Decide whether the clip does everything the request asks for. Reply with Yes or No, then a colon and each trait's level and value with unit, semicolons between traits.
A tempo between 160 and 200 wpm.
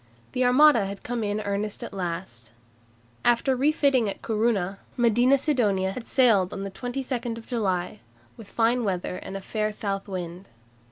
No: average, 150 wpm